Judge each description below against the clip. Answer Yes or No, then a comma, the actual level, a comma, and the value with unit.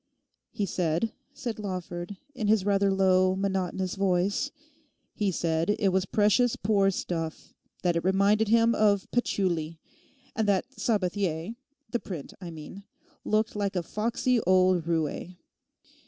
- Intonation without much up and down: No, average, 3.0 semitones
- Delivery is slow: Yes, slow, 125 wpm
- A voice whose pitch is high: Yes, high, 195 Hz